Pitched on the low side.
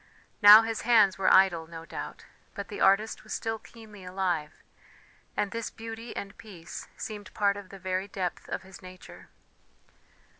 No: high, 200 Hz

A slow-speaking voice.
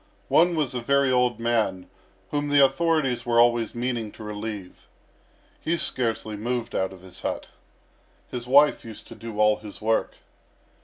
No: average, 160 wpm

